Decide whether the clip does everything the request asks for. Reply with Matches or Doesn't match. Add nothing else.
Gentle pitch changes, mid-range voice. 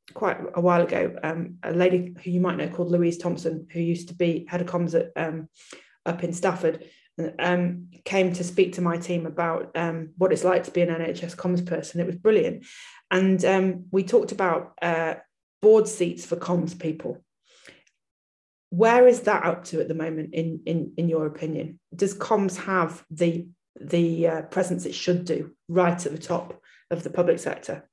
Matches